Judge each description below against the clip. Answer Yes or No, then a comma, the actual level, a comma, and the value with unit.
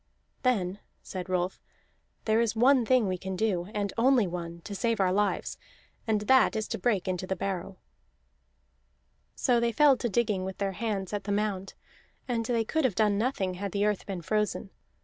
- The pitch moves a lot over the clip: No, average, 3.5 semitones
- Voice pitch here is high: Yes, high, 205 Hz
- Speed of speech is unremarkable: Yes, average, 190 wpm